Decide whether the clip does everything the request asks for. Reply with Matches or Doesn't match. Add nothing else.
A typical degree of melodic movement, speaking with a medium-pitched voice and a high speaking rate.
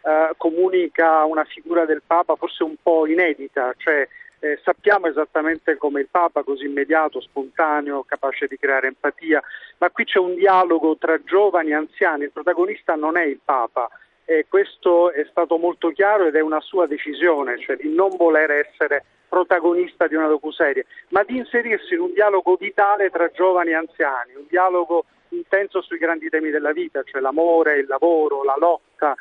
Matches